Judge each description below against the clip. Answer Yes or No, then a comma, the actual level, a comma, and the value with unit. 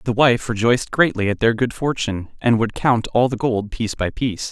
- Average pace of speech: No, fast, 225 wpm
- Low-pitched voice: Yes, low, 115 Hz